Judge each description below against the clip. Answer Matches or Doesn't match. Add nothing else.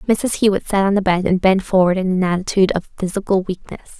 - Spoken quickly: Matches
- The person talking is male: Doesn't match